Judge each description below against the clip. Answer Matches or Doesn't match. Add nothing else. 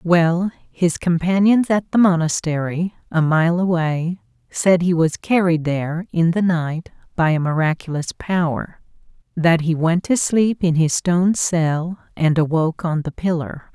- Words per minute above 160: Doesn't match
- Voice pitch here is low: Doesn't match